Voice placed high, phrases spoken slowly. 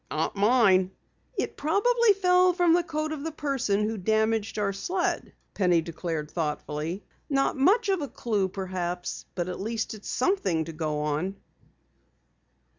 No: high, 210 Hz; average, 150 wpm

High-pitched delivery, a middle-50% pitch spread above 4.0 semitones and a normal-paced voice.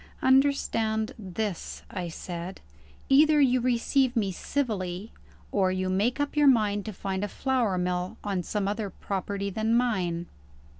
Yes: high, 210 Hz; average, 4.8 semitones; average, 145 wpm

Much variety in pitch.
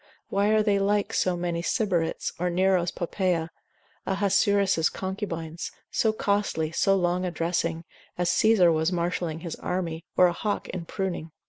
No: average, 2.8 semitones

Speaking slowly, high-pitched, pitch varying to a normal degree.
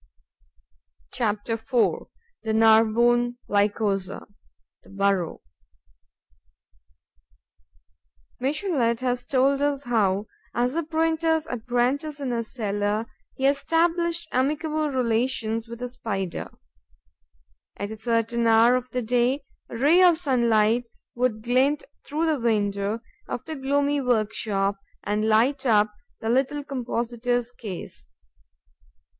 Yes: slow, 110 wpm; high, 240 Hz; average, 4.0 semitones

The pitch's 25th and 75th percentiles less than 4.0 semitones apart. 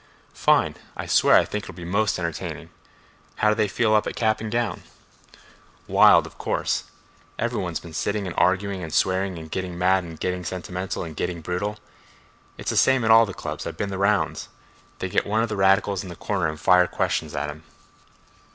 Yes: average, 3.2 semitones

